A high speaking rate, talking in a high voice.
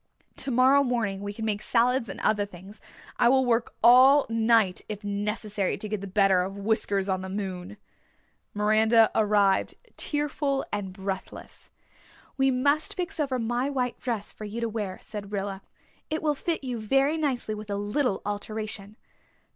No: average, 165 wpm; high, 215 Hz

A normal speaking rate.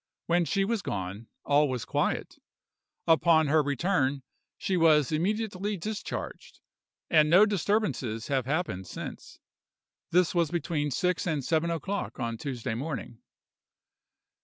No: slow, 125 wpm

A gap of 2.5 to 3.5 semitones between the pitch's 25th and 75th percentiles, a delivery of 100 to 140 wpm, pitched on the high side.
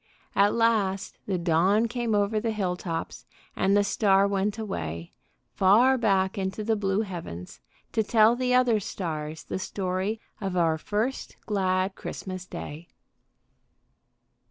Yes: average, 2.9 semitones; slow, 135 wpm; high, 195 Hz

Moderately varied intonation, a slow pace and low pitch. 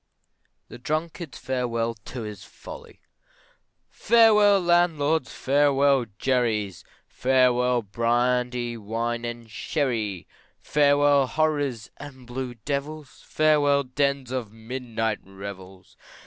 Yes: average, 3.7 semitones; slow, 90 wpm; low, 125 Hz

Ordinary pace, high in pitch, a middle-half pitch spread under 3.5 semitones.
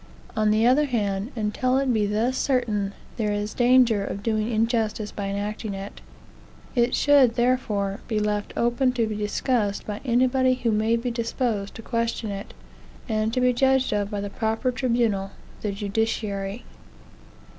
Yes: average, 160 wpm; high, 225 Hz; average, 3.1 semitones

